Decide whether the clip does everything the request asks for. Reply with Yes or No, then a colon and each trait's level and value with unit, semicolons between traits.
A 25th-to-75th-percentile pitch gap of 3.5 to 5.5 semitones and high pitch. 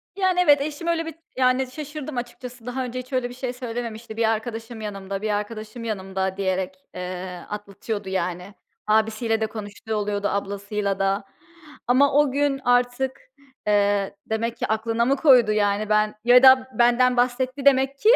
Yes: average, 3.9 semitones; high, 230 Hz